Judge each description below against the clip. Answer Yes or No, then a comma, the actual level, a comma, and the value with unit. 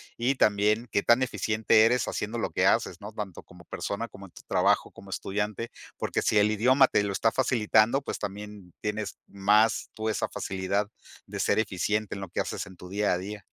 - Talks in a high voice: No, low, 105 Hz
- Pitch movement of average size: No, narrow, 2.1 semitones